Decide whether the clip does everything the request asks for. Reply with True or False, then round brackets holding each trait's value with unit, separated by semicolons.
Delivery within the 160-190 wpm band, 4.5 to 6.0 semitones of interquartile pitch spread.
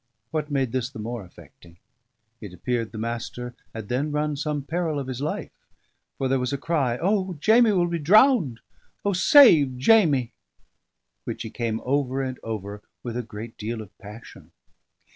True (170 wpm; 5.1 semitones)